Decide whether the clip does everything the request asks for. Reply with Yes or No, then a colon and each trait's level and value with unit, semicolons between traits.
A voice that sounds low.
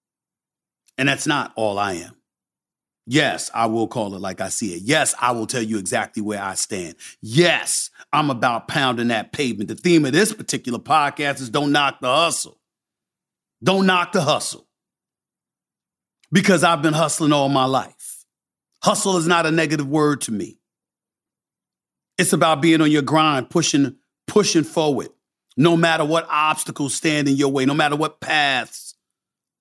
No: medium, 150 Hz